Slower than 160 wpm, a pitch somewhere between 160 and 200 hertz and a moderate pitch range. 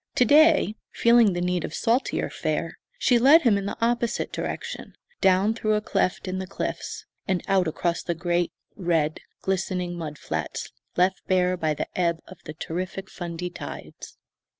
No: average, 170 wpm; medium, 185 Hz; average, 3.7 semitones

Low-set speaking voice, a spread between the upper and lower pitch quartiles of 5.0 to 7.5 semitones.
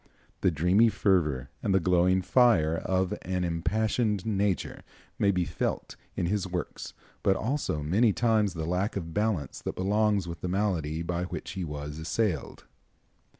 No: very low, 95 Hz; average, 3.8 semitones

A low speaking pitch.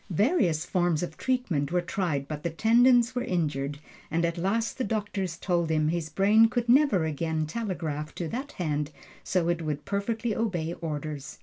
No: medium, 175 Hz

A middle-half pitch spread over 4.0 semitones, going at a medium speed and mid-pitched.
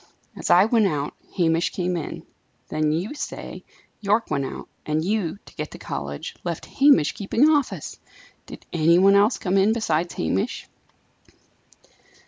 Yes: wide, 5.4 semitones; average, 150 wpm; medium, 180 Hz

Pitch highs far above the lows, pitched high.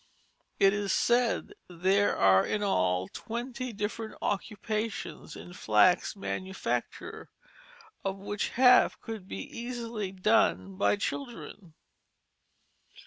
No: average, 3.5 semitones; high, 205 Hz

